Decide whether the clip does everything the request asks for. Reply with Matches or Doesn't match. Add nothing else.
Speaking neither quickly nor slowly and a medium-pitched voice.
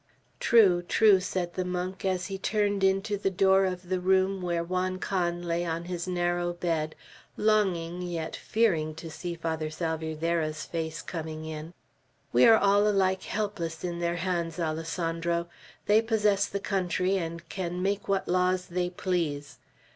Matches